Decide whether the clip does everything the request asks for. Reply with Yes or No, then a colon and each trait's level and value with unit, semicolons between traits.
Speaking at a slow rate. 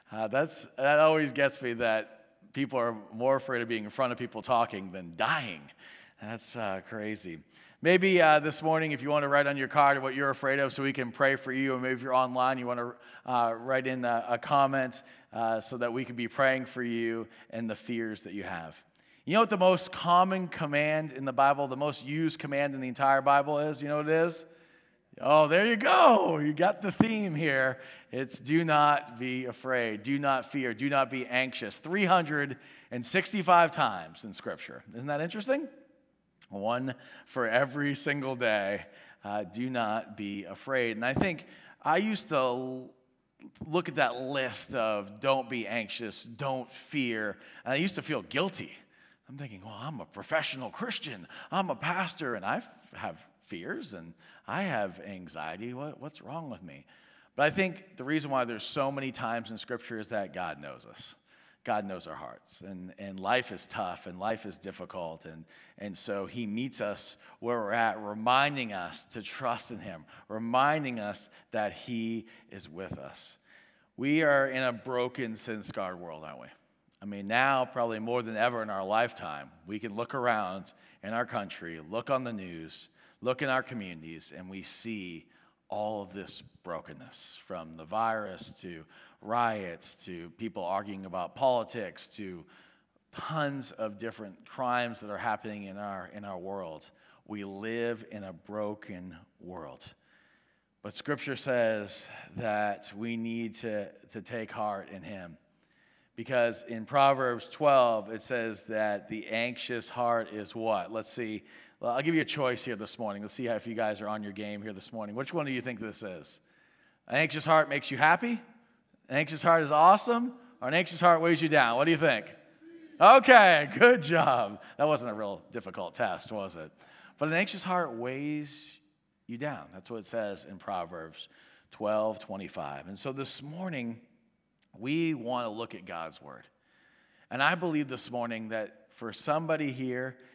No: average, 180 wpm